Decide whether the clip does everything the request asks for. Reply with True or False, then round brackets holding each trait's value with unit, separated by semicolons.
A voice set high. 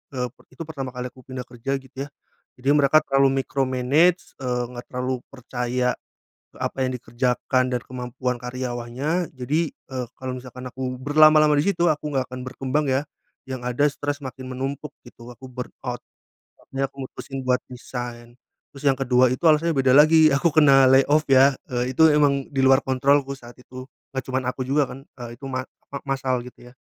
False (130 Hz)